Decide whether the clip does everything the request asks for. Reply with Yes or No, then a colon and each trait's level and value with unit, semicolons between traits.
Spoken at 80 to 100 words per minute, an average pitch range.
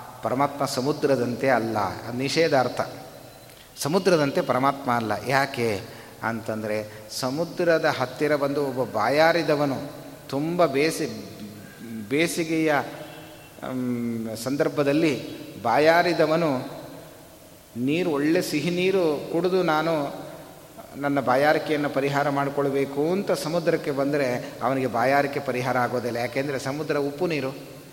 Yes: average, 85 wpm; average, 3.7 semitones